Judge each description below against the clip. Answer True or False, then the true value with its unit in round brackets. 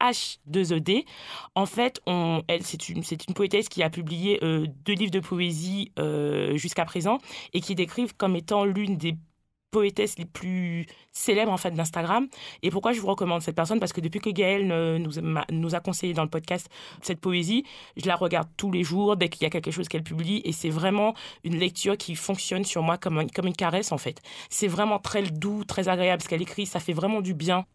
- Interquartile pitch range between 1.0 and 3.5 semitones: True (3.2 semitones)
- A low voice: False (180 Hz)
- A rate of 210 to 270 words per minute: True (220 wpm)